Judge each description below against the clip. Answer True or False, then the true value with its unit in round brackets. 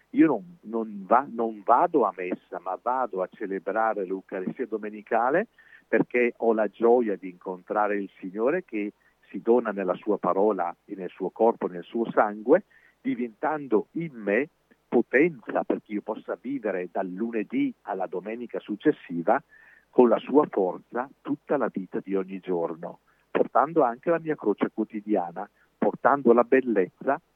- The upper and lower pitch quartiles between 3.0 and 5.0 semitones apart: True (3.8 semitones)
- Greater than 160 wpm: False (145 wpm)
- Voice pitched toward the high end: False (110 Hz)